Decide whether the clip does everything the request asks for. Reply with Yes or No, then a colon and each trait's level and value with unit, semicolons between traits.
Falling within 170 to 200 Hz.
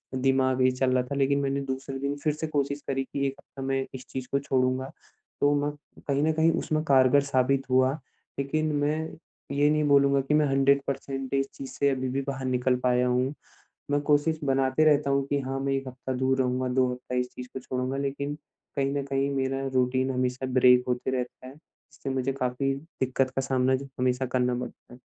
No: low, 135 Hz